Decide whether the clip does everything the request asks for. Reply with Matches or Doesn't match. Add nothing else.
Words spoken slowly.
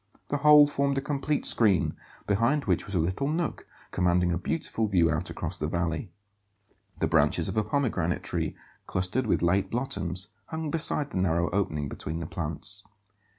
Doesn't match